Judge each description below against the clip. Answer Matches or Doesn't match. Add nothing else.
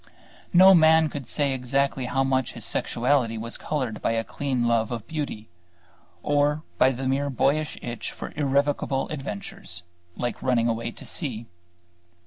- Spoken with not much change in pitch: Doesn't match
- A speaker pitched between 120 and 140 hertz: Matches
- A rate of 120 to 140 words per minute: Doesn't match